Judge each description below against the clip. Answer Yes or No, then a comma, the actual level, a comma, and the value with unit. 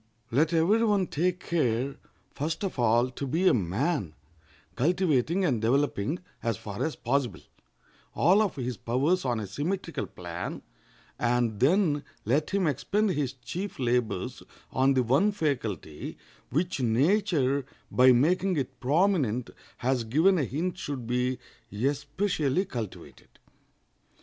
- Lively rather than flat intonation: Yes, wide, 6.2 semitones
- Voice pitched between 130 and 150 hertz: Yes, medium, 140 Hz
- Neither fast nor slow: No, slow, 130 wpm